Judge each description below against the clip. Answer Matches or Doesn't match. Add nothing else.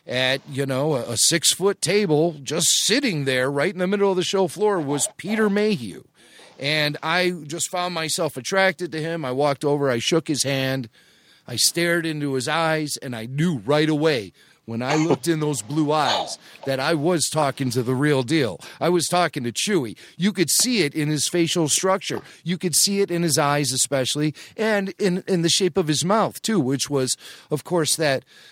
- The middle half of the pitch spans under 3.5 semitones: Doesn't match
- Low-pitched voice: Doesn't match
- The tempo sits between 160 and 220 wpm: Matches